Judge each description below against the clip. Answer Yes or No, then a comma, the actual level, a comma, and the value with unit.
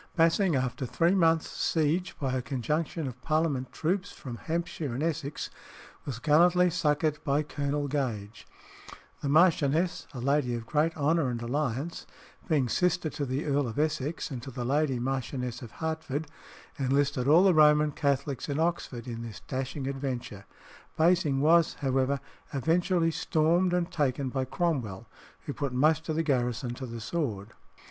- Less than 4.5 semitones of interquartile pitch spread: Yes, average, 3.8 semitones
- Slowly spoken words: No, average, 155 wpm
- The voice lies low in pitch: No, medium, 145 Hz